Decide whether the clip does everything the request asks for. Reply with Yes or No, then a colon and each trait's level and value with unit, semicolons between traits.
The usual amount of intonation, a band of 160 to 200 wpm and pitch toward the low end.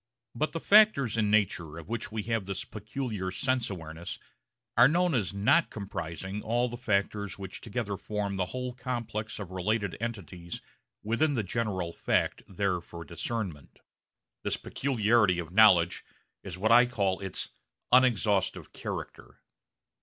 No: average, 4.0 semitones; average, 145 wpm; low, 105 Hz